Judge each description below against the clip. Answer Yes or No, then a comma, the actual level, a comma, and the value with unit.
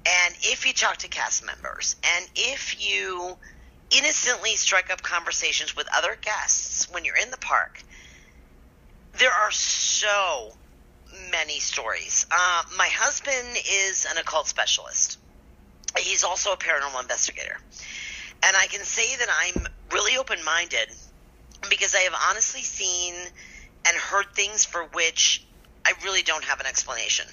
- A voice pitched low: No, medium, 180 Hz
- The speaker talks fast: No, average, 140 wpm